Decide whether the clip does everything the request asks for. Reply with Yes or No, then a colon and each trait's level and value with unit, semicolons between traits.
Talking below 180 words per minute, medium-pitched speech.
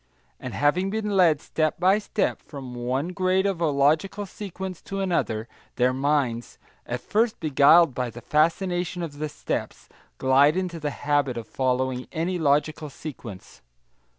Yes: average, 150 wpm; medium, 155 Hz